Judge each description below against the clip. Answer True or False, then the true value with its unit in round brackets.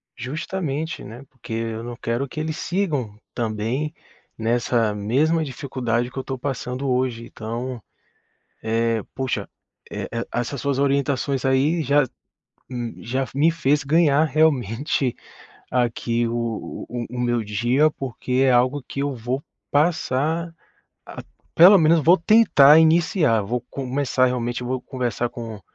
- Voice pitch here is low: True (130 Hz)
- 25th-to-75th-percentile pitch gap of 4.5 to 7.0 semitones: False (3.6 semitones)